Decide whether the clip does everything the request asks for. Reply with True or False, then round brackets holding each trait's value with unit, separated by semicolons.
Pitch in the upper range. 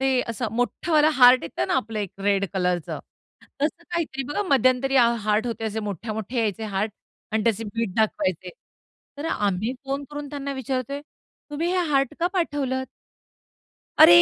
True (245 Hz)